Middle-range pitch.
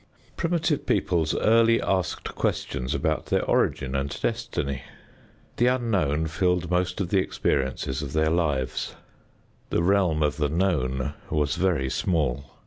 No: very low, 80 Hz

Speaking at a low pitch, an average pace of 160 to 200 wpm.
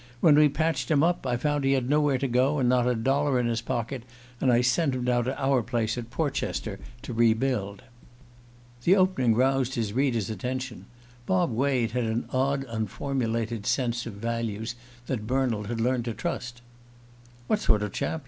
Yes: low, 125 Hz; average, 185 wpm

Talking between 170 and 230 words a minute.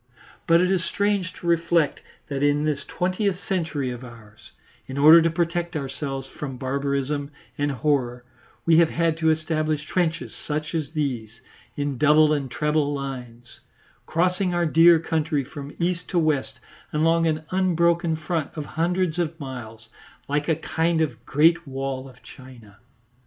No: average, 155 wpm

